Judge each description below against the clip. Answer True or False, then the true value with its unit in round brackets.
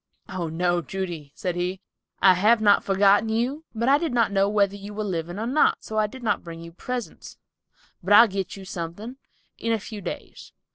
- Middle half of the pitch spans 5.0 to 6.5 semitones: False (3.8 semitones)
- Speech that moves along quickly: True (220 wpm)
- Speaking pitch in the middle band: False (200 Hz)